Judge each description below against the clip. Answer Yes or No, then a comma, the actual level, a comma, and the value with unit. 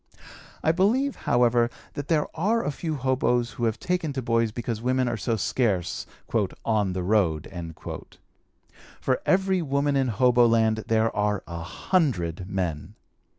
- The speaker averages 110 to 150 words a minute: Yes, average, 145 wpm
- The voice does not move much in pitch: No, wide, 5.4 semitones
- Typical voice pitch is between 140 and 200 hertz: No, low, 120 Hz